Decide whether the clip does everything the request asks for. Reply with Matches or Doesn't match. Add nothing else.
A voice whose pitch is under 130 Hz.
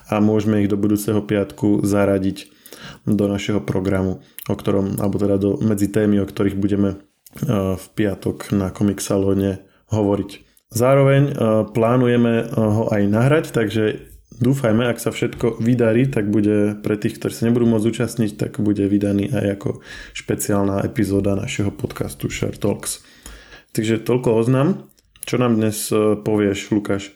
Matches